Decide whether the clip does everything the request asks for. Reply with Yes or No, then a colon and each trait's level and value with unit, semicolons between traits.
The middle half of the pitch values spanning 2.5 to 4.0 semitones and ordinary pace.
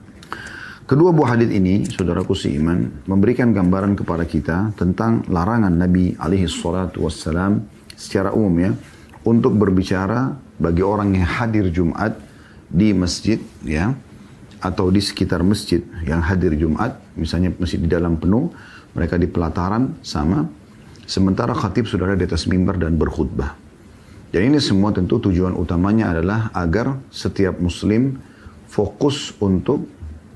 Yes: average, 3.5 semitones; average, 130 wpm